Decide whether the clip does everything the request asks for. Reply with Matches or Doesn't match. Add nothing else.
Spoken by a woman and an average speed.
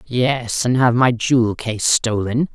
Matches